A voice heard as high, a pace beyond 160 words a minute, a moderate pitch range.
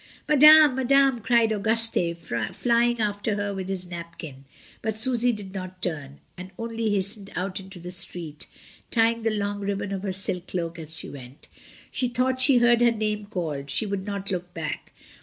Yes: high, 200 Hz; average, 175 wpm; average, 4.3 semitones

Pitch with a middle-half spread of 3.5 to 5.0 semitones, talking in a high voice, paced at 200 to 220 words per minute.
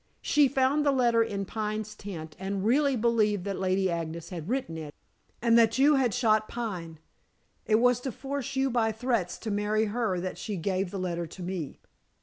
No: average, 4.7 semitones; high, 215 Hz; average, 190 wpm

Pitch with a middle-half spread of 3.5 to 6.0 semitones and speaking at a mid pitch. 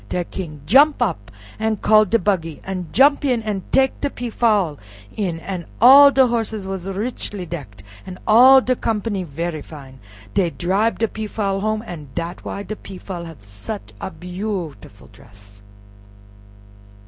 No: average, 4.9 semitones; high, 195 Hz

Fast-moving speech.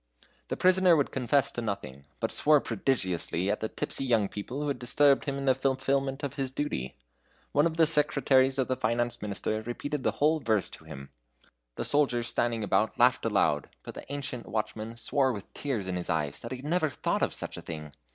Yes: fast, 210 wpm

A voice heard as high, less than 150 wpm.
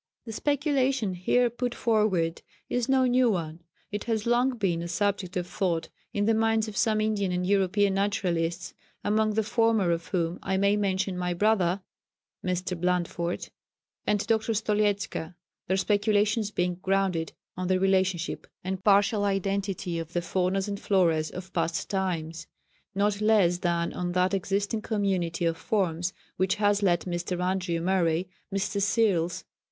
No: high, 195 Hz; average, 155 wpm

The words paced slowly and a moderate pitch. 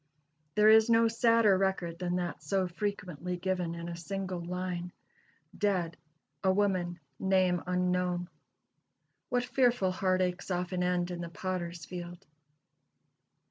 Yes: slow, 130 wpm; medium, 180 Hz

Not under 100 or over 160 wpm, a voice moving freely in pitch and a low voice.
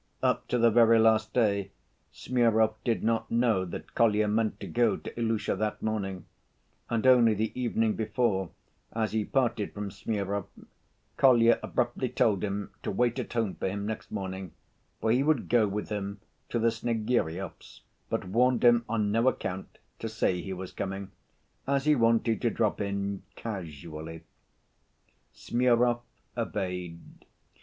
No: average, 150 wpm; average, 2.9 semitones; low, 110 Hz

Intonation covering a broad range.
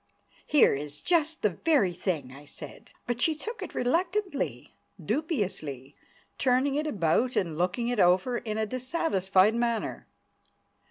Yes: wide, 8.5 semitones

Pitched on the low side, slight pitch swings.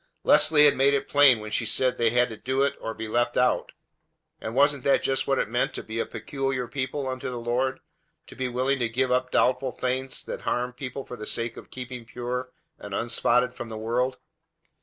Yes: low, 125 Hz; narrow, 1.9 semitones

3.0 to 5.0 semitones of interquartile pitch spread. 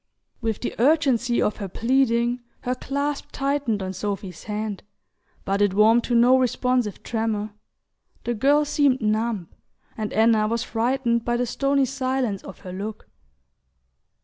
Yes: average, 3.4 semitones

